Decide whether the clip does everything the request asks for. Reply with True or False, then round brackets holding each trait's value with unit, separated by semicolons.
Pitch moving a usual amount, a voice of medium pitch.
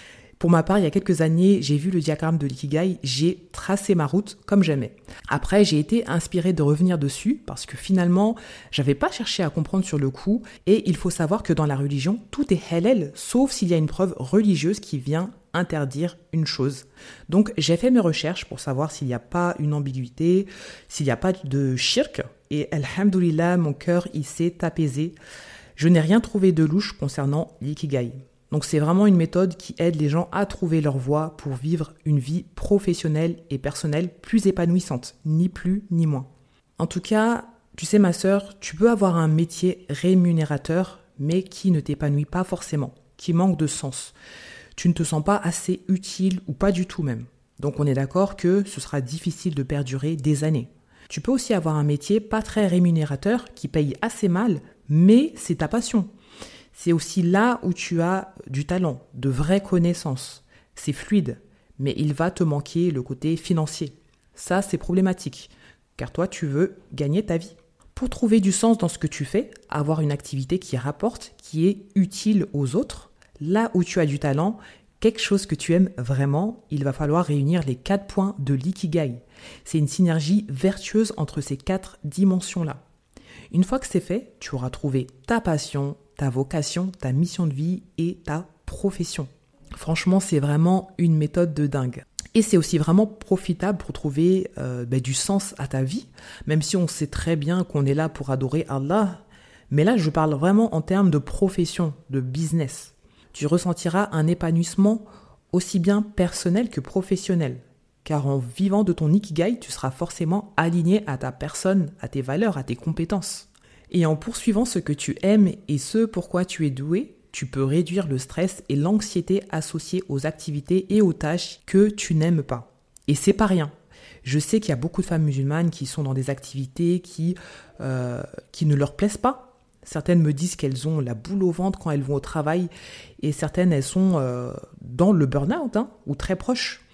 True (4.5 semitones; 170 Hz)